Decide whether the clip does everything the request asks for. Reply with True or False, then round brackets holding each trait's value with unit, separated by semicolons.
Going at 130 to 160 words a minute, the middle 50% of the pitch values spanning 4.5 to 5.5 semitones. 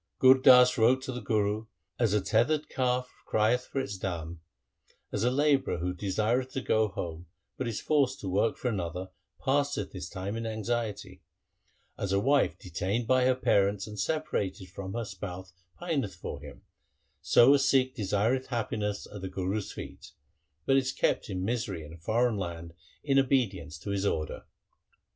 False (175 wpm; 5.2 semitones)